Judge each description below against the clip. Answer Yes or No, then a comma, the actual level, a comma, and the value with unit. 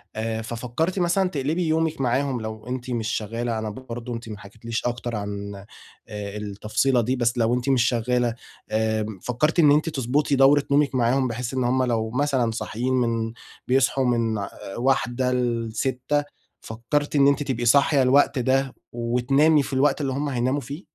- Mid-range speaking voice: No, low, 125 Hz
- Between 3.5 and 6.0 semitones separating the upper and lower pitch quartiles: No, average, 3.1 semitones